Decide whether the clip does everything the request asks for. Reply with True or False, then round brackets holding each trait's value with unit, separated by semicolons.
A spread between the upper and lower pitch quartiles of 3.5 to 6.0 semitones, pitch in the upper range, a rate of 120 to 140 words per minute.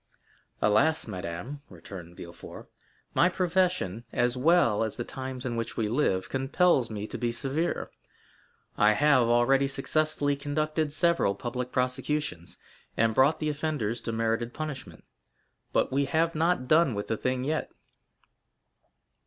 False (5.2 semitones; 130 Hz; 135 wpm)